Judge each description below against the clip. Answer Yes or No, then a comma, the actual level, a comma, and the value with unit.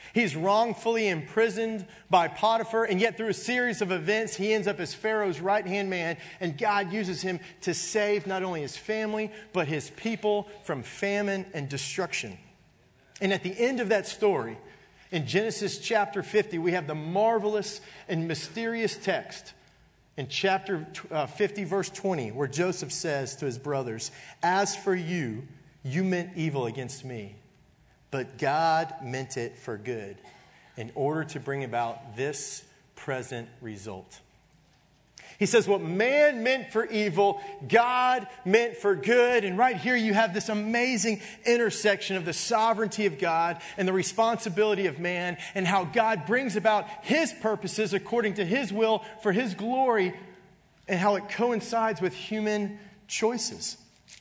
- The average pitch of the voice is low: No, high, 195 Hz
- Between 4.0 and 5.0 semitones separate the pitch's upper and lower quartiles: Yes, average, 4.7 semitones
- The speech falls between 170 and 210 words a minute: No, average, 155 wpm